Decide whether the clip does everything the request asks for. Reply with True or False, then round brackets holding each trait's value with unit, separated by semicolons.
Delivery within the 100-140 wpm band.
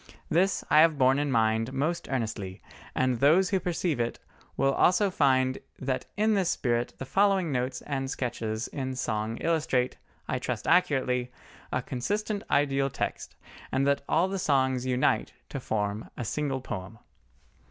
False (155 wpm)